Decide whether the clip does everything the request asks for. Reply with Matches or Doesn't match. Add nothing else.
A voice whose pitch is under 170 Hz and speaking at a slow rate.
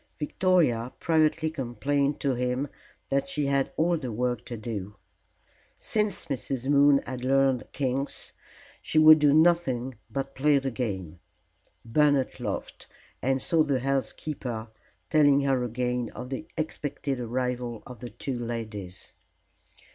Matches